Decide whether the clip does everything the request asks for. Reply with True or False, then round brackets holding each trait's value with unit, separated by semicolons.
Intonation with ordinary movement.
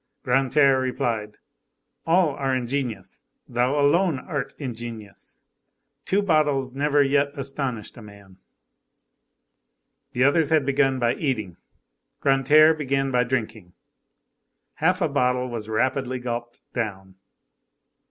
True (3.2 semitones)